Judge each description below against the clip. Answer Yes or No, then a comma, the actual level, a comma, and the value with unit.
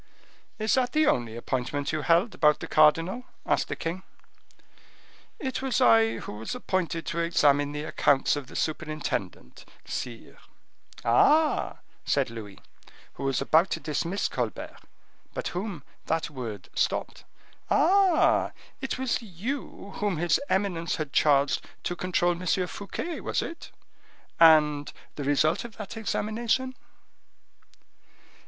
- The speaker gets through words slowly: Yes, slow, 130 wpm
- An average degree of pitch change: No, wide, 6.6 semitones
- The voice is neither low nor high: Yes, medium, 165 Hz